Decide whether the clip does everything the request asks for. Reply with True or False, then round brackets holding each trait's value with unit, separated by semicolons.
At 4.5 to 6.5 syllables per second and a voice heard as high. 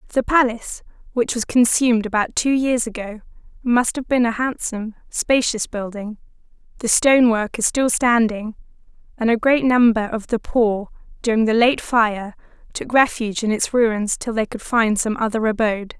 True (5.0 syllables/s; 230 Hz)